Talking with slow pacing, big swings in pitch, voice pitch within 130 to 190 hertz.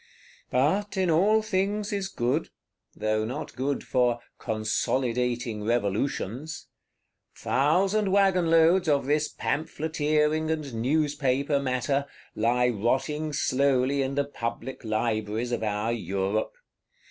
No: slow, 105 wpm; average, 4.9 semitones; low, 135 Hz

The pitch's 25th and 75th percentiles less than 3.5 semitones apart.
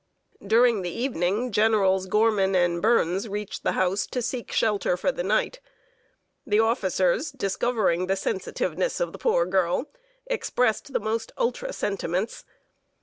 No: average, 4.0 semitones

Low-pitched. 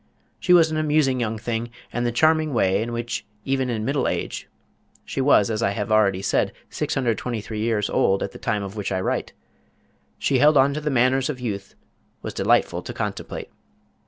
Yes: low, 120 Hz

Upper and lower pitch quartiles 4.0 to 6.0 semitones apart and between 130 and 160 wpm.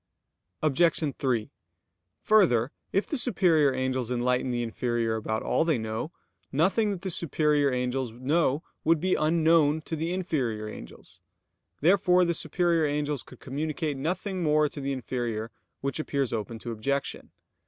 Yes: average, 5.0 semitones; average, 145 wpm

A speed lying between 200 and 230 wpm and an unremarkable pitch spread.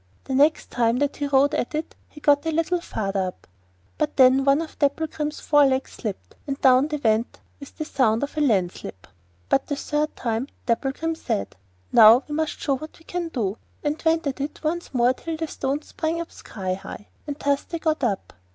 Yes: fast, 205 wpm; average, 4.1 semitones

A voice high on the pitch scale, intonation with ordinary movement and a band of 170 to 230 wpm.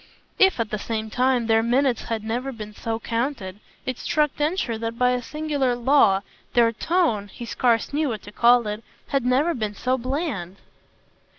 Yes: high, 240 Hz; average, 3.5 semitones; average, 180 wpm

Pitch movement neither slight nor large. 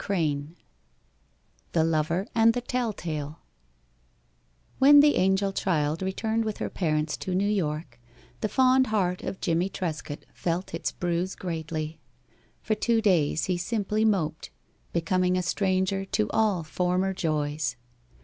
Yes: average, 4.3 semitones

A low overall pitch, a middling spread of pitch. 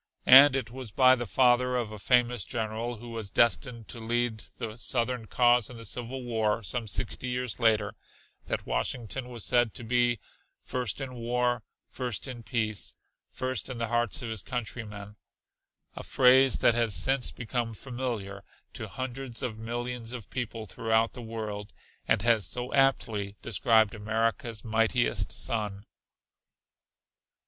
No: low, 120 Hz; narrow, 2.2 semitones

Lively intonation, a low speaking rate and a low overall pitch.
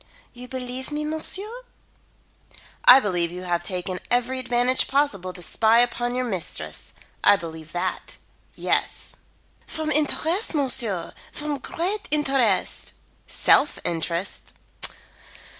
No: wide, 8.1 semitones; slow, 115 wpm; high, 245 Hz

